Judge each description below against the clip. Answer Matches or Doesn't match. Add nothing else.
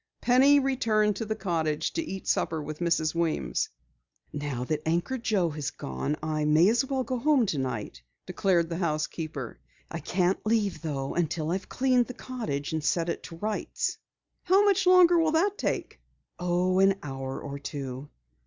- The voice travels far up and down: Matches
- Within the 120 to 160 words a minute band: Doesn't match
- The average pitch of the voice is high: Doesn't match